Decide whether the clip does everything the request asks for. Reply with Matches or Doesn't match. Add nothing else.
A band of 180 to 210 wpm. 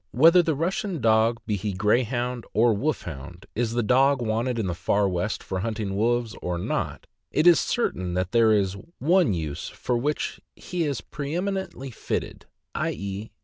Matches